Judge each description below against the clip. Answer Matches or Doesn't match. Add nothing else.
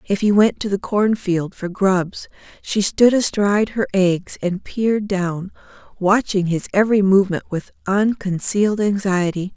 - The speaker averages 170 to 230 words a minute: Doesn't match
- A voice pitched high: Matches